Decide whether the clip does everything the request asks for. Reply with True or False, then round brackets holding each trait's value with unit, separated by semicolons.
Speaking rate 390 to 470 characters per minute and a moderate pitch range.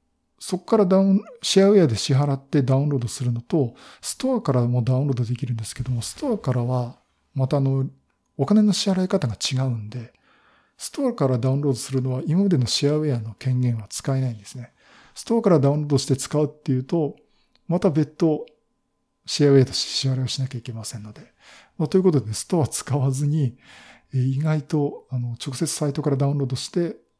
True (415 characters per minute; 3.8 semitones)